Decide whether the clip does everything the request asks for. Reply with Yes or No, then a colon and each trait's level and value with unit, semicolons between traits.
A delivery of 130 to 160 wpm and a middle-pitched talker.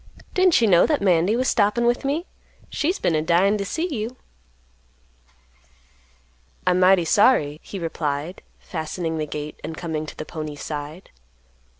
Yes: average, 155 wpm; medium, 180 Hz